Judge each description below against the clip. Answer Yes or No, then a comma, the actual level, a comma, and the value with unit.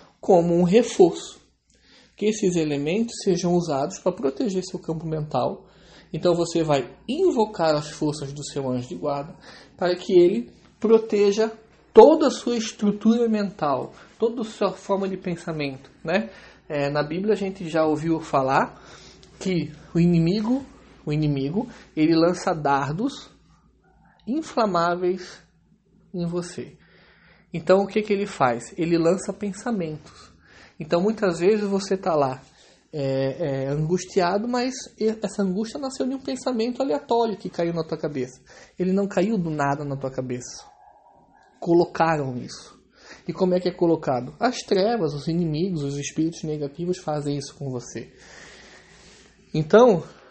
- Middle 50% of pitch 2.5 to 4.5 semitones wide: No, average, 5.2 semitones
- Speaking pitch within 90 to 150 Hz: No, medium, 180 Hz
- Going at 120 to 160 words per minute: Yes, average, 140 wpm